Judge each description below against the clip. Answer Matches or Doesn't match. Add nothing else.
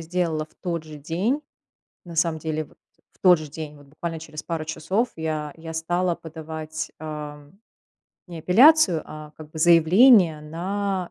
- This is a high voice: Doesn't match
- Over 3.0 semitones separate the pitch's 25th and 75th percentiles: Doesn't match